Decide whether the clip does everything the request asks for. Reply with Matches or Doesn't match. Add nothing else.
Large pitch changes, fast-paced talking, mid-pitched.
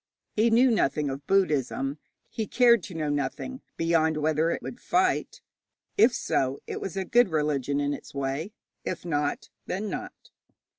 Doesn't match